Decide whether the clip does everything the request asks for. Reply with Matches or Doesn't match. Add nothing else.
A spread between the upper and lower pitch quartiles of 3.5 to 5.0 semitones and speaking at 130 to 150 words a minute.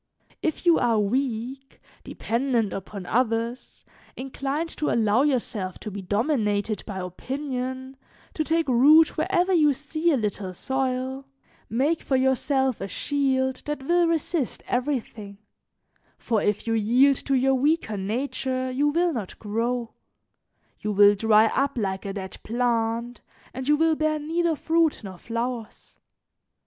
Matches